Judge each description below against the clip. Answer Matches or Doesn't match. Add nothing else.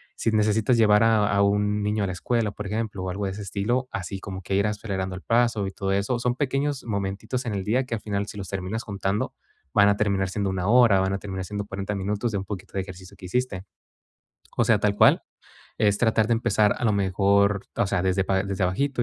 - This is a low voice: Matches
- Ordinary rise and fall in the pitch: Doesn't match